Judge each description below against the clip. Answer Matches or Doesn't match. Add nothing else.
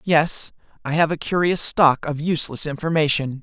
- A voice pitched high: Doesn't match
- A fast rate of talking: Doesn't match